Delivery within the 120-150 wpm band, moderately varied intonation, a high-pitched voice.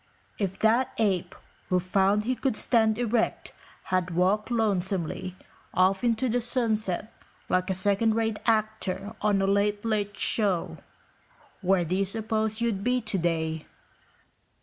Yes: slow, 135 wpm; average, 3.0 semitones; high, 205 Hz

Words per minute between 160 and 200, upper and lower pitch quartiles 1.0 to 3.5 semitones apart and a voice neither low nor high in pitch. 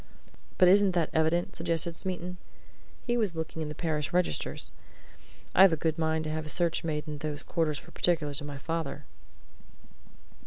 Yes: average, 170 wpm; narrow, 2.4 semitones; medium, 160 Hz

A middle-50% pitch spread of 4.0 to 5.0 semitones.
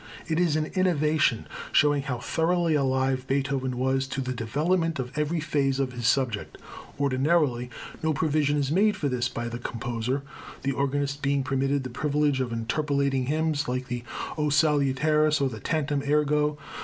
No: average, 2.8 semitones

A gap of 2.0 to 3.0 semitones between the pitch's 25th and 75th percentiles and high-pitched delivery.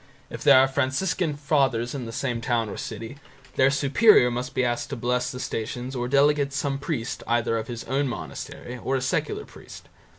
No: narrow, 2.6 semitones; low, 130 Hz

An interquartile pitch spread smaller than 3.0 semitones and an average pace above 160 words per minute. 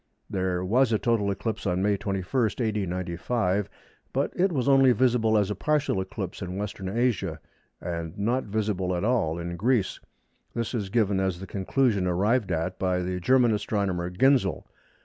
No: average, 4.2 semitones; average, 170 wpm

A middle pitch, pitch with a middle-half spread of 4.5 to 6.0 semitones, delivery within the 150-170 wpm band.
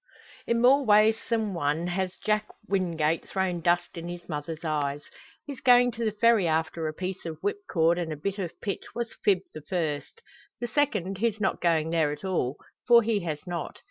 No: medium, 180 Hz; average, 5.2 semitones; average, 195 wpm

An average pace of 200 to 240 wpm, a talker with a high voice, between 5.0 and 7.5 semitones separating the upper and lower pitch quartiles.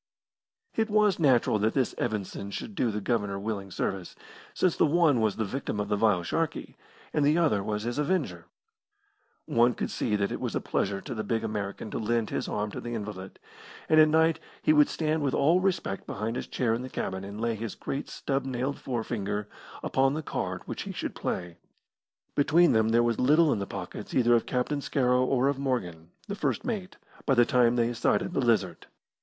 No: fast, 205 wpm; low, 120 Hz; wide, 5.6 semitones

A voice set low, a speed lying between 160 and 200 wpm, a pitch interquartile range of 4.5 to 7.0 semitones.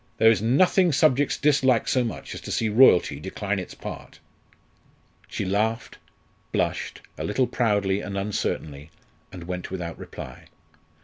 No: low, 105 Hz; average, 140 wpm; average, 5.3 semitones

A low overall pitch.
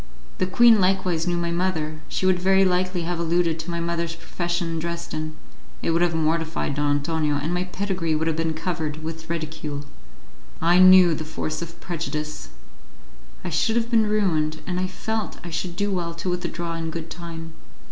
No: medium, 170 Hz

